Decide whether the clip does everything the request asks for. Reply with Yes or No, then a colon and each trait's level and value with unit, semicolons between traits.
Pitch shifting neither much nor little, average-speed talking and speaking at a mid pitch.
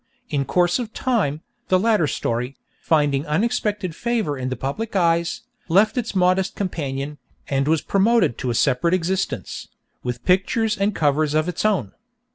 No: wide, 6.3 semitones; average, 155 wpm; medium, 170 Hz